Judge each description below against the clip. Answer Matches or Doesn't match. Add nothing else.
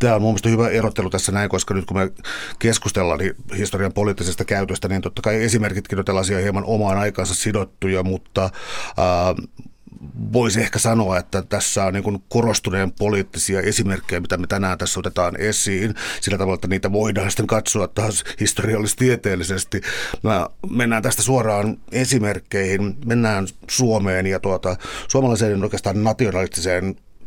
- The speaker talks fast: Doesn't match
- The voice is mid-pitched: Doesn't match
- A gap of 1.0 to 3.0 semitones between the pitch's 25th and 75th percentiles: Matches